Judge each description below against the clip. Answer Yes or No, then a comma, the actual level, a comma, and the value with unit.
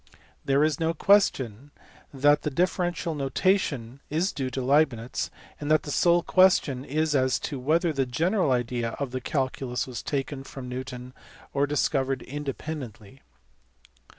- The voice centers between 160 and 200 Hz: No, medium, 140 Hz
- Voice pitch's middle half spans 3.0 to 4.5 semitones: Yes, average, 3.4 semitones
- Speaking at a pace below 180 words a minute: Yes, average, 140 wpm